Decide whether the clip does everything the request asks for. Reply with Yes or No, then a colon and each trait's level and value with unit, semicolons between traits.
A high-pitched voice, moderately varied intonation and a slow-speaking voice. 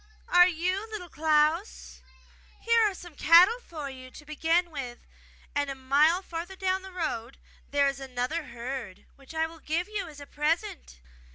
No: very high, 320 Hz; average, 4.5 semitones; average, 170 wpm